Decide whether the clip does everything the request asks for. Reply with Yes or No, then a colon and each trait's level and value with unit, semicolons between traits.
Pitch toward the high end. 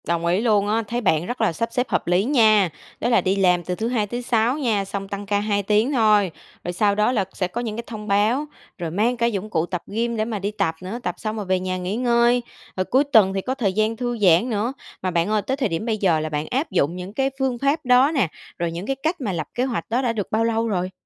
Yes: high, 215 Hz